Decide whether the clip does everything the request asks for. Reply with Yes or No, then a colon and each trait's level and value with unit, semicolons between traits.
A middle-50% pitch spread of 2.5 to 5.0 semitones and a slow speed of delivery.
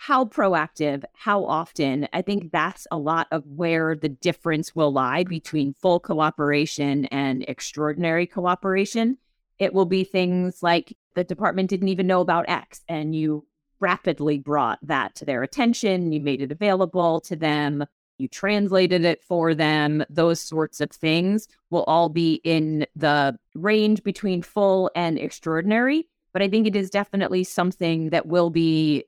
No: average, 3.7 semitones; average, 155 wpm